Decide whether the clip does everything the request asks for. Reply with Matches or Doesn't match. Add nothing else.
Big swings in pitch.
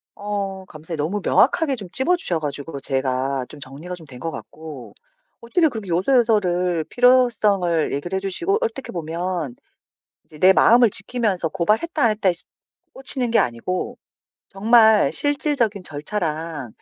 Matches